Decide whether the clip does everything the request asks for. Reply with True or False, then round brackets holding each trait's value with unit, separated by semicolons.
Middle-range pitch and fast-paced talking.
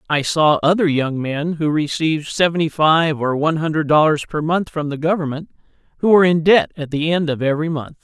True (155 Hz; 210 wpm)